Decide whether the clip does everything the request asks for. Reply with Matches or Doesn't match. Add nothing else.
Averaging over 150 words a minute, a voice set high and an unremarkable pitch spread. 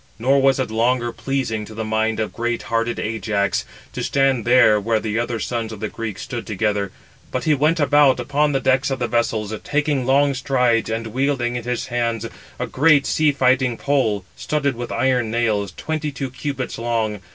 Doesn't match